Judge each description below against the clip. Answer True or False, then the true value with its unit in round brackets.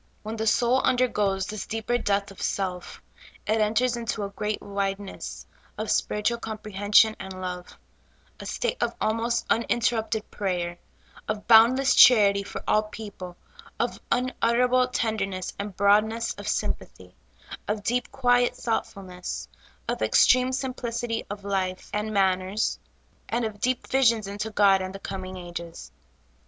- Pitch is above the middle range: True (215 Hz)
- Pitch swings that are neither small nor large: True (3.1 semitones)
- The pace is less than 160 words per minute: True (140 wpm)